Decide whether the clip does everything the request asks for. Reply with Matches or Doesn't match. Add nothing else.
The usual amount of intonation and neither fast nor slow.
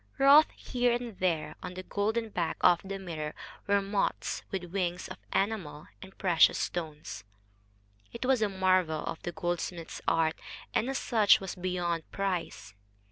Matches